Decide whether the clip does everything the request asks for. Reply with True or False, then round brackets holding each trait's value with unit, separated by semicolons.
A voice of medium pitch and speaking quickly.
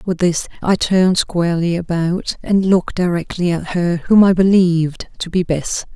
False (175 Hz; 170 wpm)